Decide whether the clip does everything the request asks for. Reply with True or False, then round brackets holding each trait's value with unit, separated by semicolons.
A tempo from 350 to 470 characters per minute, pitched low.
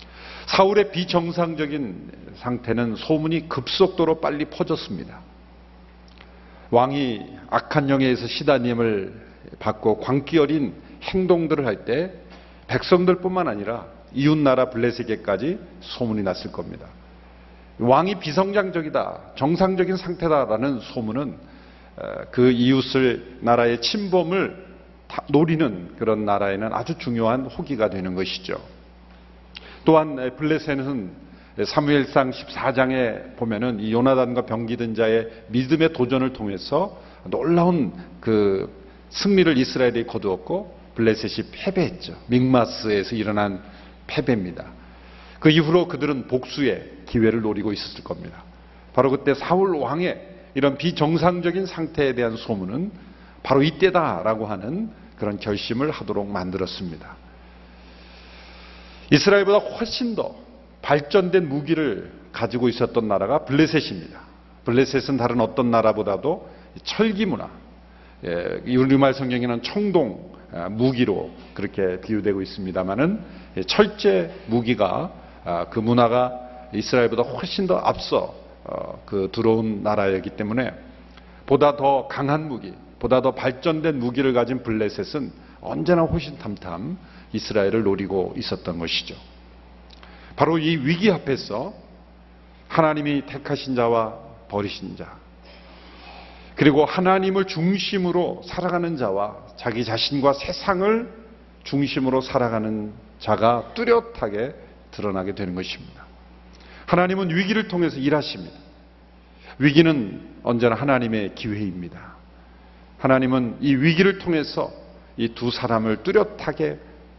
False (275 characters per minute; 125 Hz)